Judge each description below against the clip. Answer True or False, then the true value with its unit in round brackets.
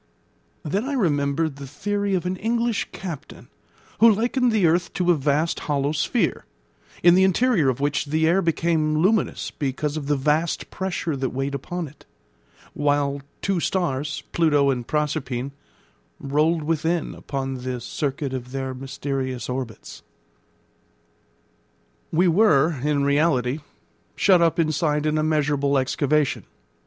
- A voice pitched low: False (150 Hz)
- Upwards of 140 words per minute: False (135 wpm)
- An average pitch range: True (3.8 semitones)